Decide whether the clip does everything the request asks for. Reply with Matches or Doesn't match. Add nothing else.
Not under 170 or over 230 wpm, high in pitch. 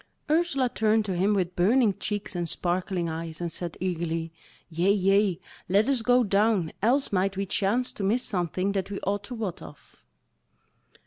Matches